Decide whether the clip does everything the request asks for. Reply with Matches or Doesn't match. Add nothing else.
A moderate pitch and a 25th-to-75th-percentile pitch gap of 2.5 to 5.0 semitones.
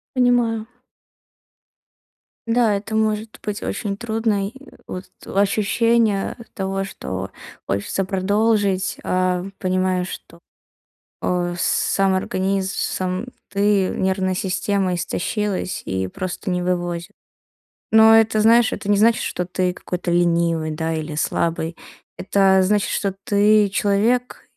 Doesn't match